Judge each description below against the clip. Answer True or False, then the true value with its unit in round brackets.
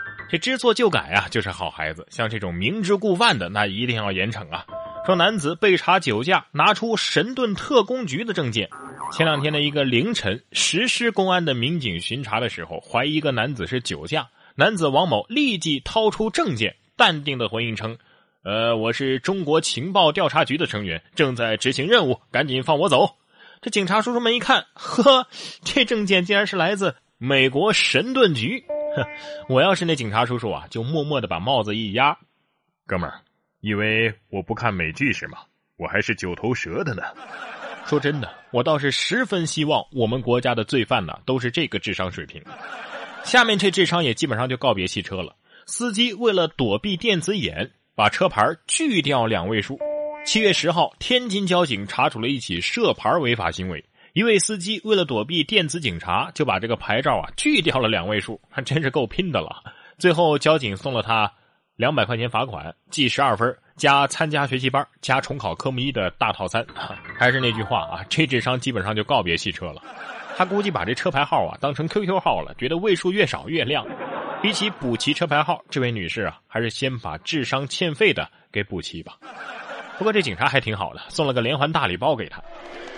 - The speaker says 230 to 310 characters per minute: True (290 characters per minute)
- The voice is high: False (140 Hz)